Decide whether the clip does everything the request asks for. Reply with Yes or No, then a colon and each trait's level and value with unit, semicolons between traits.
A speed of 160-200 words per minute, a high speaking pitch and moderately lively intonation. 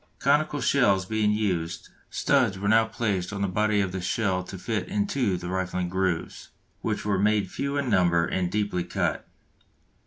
No: average, 175 wpm; low, 100 Hz; average, 3.3 semitones